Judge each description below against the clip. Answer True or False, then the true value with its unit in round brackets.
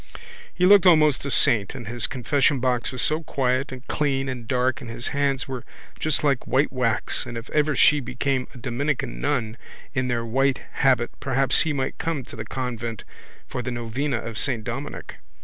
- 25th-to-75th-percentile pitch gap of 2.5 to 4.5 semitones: True (2.9 semitones)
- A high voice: False (130 Hz)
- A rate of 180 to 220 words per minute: True (185 wpm)